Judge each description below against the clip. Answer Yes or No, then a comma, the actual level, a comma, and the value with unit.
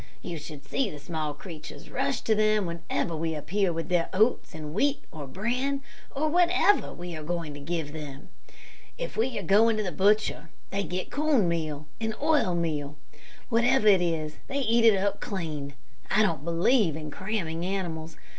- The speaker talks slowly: No, average, 180 wpm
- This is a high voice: No, medium, 175 Hz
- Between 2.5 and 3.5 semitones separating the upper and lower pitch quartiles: No, wide, 5.5 semitones